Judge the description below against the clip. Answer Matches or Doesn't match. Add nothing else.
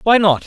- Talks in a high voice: Matches